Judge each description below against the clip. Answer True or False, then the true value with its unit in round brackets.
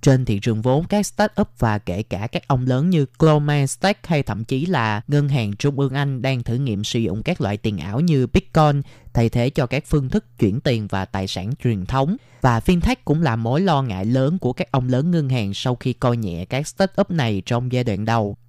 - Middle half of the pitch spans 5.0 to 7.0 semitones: False (4.6 semitones)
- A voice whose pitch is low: True (130 Hz)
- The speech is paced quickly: False (235 wpm)